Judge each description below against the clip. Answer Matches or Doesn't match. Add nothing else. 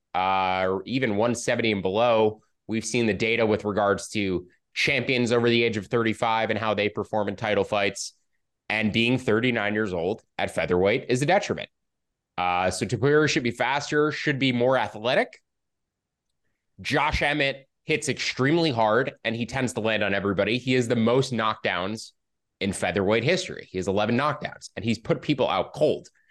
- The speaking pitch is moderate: Doesn't match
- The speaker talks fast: Doesn't match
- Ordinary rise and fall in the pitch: Matches